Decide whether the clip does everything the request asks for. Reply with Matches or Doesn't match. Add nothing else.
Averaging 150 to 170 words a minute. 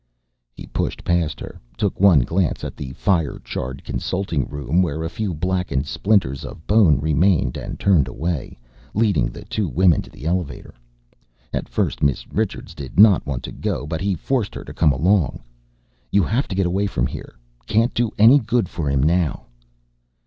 Doesn't match